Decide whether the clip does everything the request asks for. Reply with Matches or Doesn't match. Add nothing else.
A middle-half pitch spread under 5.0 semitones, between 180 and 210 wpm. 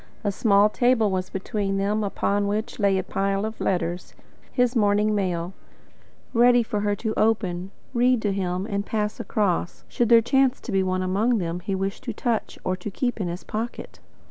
Matches